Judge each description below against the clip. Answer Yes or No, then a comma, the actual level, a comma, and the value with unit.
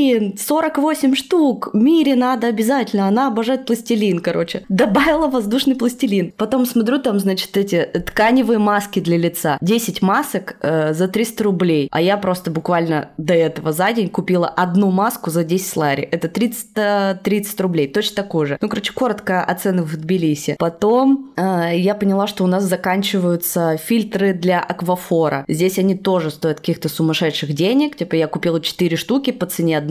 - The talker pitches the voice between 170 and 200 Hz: Yes, high, 190 Hz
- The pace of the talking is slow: No, fast, 160 wpm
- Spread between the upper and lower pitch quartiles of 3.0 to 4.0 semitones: No, average, 5.1 semitones